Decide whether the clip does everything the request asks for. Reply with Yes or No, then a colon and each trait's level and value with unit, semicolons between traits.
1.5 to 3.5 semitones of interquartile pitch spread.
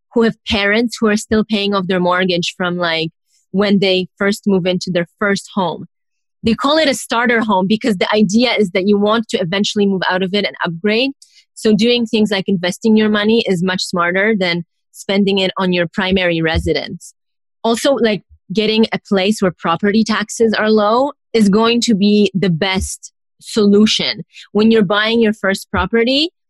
Yes: average, 3.1 semitones